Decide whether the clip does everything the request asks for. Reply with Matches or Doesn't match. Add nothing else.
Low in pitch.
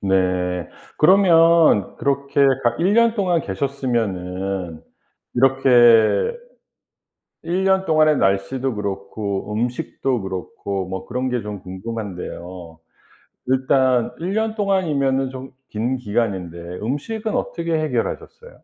Matches